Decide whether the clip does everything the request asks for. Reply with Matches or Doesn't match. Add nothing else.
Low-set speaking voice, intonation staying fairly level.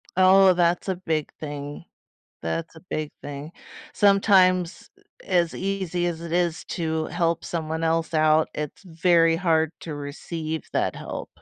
Doesn't match